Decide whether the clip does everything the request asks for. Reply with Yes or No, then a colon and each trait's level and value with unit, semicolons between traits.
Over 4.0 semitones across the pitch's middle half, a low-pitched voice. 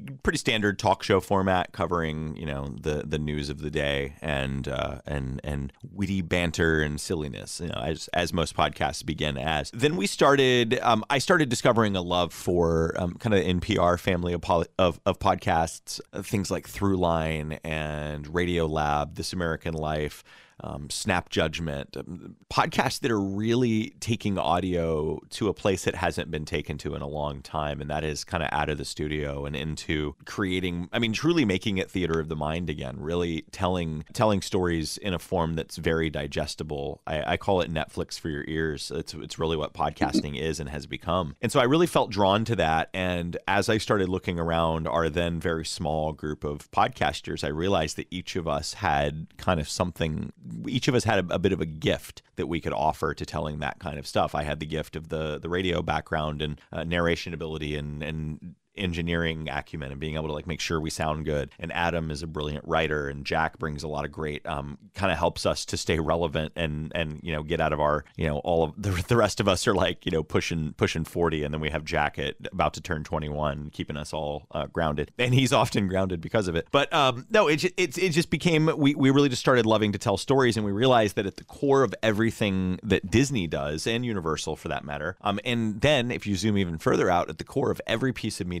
Yes: average, 4.6 semitones; very low, 85 Hz